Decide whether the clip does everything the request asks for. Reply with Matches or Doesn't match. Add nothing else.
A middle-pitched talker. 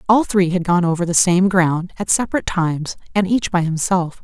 Matches